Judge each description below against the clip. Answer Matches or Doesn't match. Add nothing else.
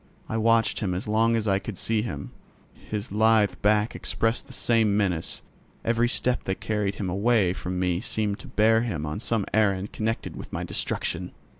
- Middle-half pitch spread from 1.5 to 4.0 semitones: Matches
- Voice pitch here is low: Matches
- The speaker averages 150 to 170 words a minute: Doesn't match